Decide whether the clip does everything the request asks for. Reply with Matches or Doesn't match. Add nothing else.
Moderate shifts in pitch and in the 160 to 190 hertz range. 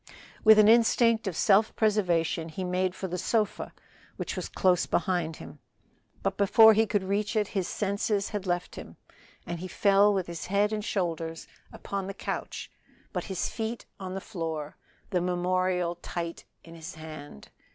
Matches